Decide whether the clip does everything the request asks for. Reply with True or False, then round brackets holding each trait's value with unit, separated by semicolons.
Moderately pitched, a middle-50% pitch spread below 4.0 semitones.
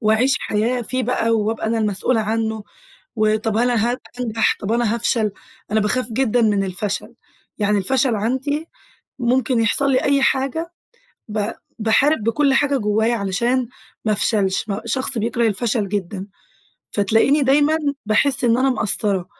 False (225 Hz; 3.3 semitones)